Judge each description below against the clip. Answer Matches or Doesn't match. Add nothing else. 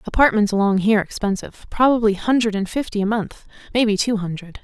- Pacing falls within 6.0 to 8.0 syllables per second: Matches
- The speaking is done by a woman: Matches